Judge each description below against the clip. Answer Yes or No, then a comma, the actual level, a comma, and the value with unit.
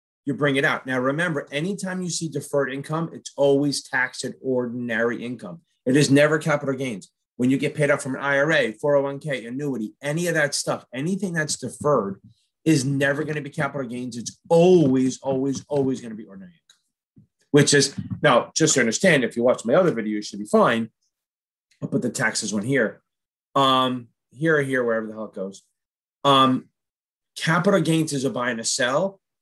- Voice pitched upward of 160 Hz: No, medium, 140 Hz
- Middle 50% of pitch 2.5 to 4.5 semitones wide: Yes, average, 3.5 semitones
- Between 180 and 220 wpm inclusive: Yes, average, 195 wpm